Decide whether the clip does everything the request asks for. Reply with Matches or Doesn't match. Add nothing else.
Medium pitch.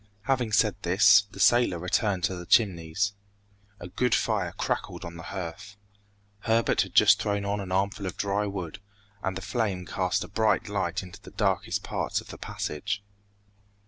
Doesn't match